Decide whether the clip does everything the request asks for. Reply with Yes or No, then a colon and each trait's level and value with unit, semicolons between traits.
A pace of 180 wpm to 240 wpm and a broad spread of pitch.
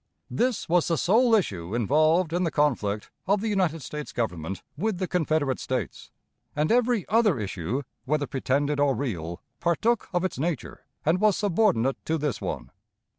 No: average, 165 wpm; wide, 6.6 semitones